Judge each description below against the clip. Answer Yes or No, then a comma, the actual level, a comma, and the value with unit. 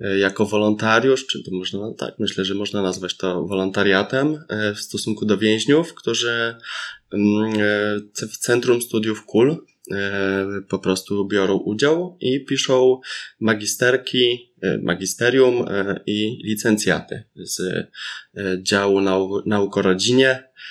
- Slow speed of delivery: Yes, slow, 100 wpm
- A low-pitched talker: Yes, low, 105 Hz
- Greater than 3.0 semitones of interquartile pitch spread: Yes, average, 3.6 semitones